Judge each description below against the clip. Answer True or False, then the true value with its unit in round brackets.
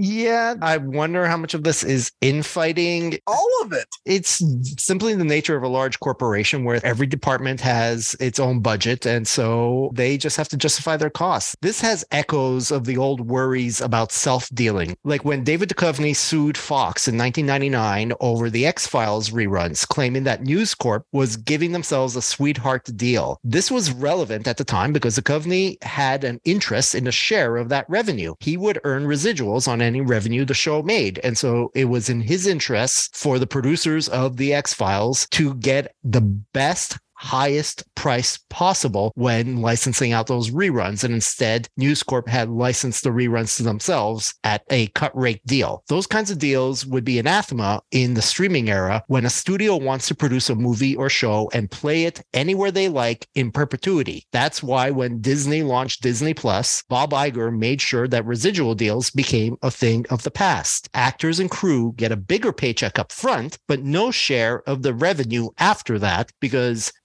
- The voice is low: True (130 Hz)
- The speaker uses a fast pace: False (185 wpm)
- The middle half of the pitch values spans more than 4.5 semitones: False (4.1 semitones)